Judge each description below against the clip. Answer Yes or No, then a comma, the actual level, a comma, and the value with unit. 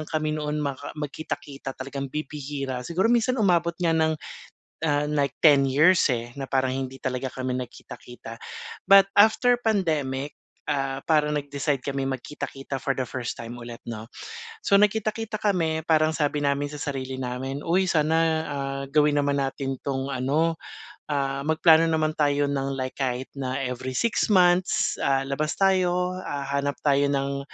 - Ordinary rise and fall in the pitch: Yes, average, 3.0 semitones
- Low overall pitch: No, medium, 145 Hz